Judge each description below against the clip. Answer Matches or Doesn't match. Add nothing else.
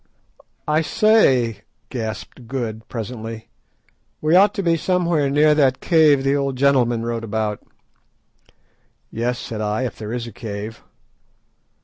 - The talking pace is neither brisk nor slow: Doesn't match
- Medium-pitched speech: Doesn't match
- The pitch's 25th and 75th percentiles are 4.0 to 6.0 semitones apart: Matches